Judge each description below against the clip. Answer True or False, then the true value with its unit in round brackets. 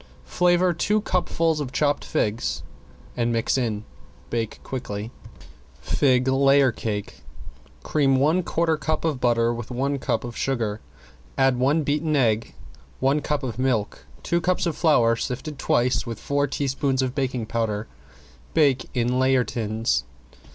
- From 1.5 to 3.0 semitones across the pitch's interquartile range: False (4.0 semitones)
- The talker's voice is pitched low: True (130 Hz)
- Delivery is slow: False (145 wpm)